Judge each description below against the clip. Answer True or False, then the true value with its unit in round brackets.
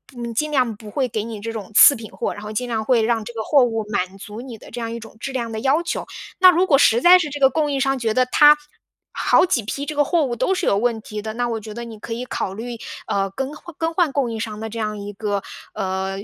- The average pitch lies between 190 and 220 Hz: False (235 Hz)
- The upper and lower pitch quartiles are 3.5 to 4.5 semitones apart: True (4.0 semitones)